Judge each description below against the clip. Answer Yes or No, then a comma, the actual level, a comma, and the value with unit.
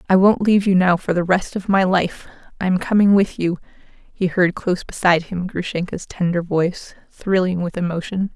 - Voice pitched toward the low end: No, medium, 185 Hz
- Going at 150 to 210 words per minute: Yes, average, 185 wpm